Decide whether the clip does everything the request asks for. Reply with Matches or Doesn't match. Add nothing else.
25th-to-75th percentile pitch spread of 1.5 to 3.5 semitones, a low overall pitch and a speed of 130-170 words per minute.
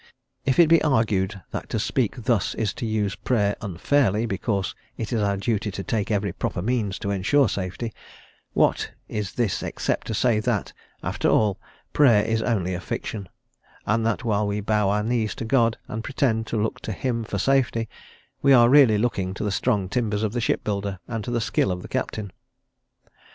Doesn't match